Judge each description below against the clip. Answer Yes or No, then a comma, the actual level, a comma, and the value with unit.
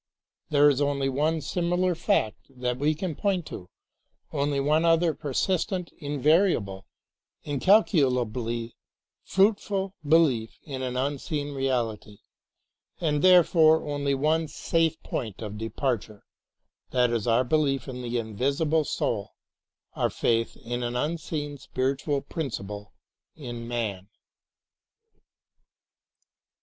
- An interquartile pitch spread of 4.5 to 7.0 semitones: Yes, average, 5.0 semitones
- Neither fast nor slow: No, slow, 115 wpm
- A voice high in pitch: No, medium, 140 Hz